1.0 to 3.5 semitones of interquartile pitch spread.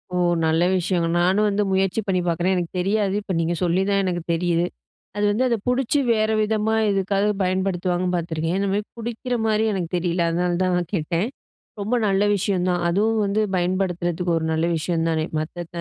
Yes: average, 2.8 semitones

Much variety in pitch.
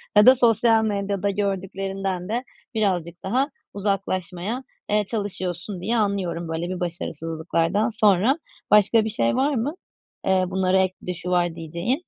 No: average, 3.3 semitones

